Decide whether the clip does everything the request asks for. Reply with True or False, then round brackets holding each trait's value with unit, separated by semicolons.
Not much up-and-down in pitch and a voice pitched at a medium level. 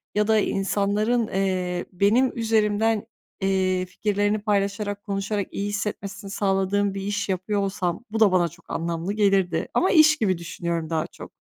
False (2.1 semitones; 200 Hz)